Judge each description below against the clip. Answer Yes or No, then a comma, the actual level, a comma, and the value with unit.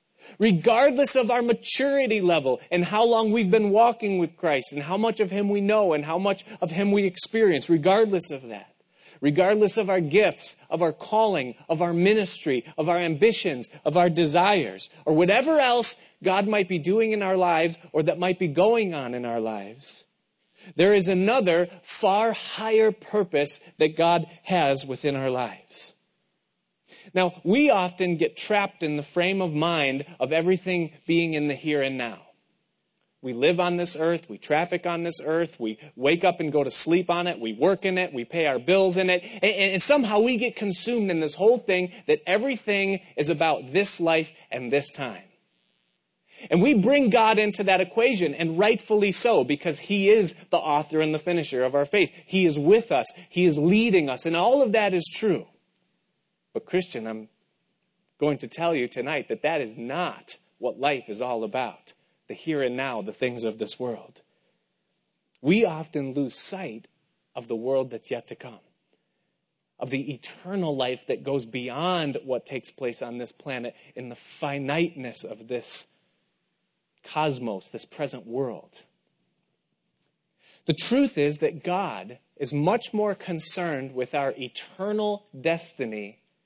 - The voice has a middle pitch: Yes, medium, 175 Hz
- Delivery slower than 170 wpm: No, average, 175 wpm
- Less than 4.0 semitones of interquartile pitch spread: No, wide, 5.4 semitones